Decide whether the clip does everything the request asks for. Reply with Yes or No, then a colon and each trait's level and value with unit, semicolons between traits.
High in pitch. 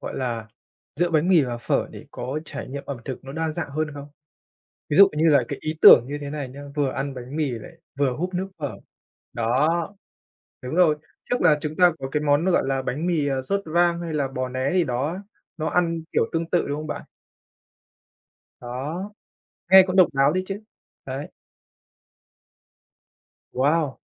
No: medium, 150 Hz